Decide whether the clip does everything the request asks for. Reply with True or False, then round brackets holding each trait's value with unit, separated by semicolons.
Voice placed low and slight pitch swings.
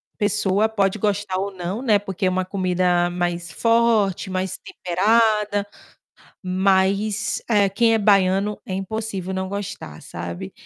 False (195 Hz; 2.2 semitones)